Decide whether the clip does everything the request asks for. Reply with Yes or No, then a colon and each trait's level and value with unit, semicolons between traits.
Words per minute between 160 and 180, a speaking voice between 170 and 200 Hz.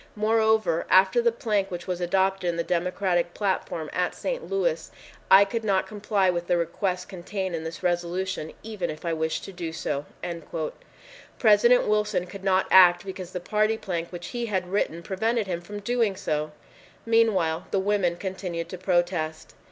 Yes: average, 170 wpm; high, 190 Hz